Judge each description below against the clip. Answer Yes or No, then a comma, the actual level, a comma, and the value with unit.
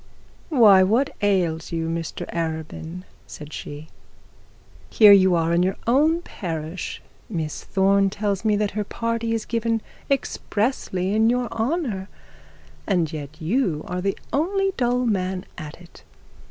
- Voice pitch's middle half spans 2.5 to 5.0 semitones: No, wide, 5.4 semitones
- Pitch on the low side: No, high, 195 Hz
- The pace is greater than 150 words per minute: No, average, 140 wpm